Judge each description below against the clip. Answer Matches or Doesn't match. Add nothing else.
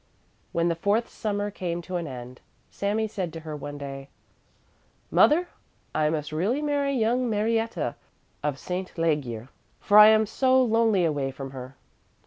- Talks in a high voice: Doesn't match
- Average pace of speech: Matches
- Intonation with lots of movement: Matches